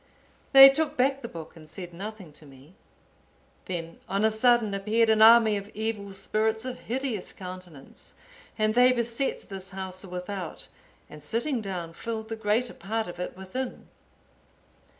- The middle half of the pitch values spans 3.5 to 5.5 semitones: Yes, average, 4.1 semitones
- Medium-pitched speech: No, high, 210 Hz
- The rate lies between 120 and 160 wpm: Yes, average, 155 wpm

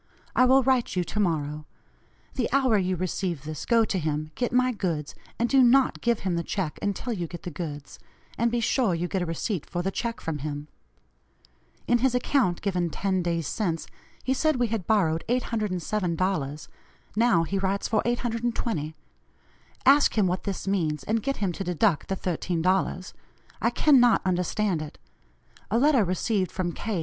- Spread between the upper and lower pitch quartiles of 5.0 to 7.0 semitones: Yes, wide, 5.5 semitones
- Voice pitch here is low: No, high, 190 Hz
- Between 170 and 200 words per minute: Yes, average, 180 wpm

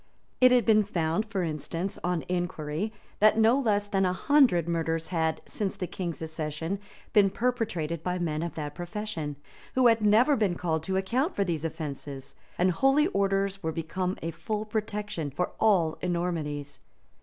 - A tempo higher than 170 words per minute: No, average, 165 wpm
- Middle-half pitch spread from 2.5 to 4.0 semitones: No, average, 4.6 semitones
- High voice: No, medium, 180 Hz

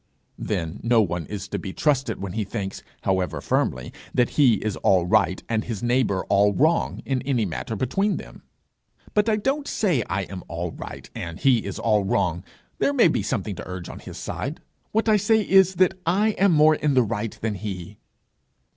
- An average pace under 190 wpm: No, average, 200 wpm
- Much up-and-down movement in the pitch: Yes, wide, 8.4 semitones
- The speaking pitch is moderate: No, low, 115 Hz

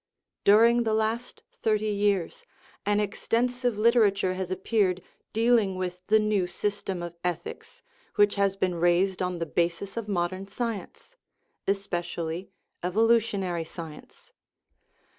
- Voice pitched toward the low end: No, high, 195 Hz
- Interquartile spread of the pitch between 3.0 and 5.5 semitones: Yes, average, 3.4 semitones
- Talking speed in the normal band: No, slow, 120 wpm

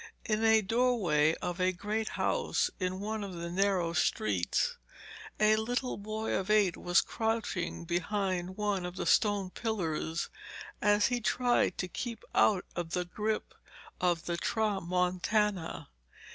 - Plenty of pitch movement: No, average, 3.5 semitones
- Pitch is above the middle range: Yes, high, 195 Hz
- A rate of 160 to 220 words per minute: No, average, 140 wpm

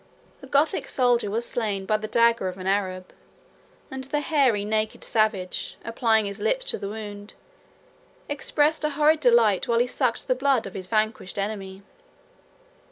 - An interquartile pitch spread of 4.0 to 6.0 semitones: Yes, average, 4.4 semitones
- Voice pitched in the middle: No, high, 220 Hz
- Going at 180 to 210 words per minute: No, average, 165 wpm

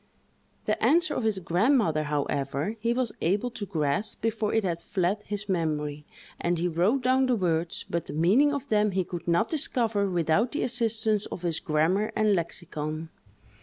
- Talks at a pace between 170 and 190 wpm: Yes, average, 175 wpm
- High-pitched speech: Yes, high, 195 Hz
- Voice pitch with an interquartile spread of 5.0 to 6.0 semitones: Yes, wide, 5.4 semitones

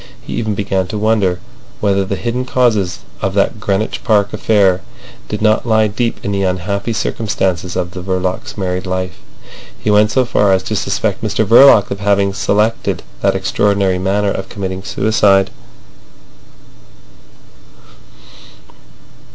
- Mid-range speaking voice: No, low, 100 Hz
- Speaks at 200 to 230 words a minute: No, average, 140 wpm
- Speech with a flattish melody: Yes, narrow, 2.3 semitones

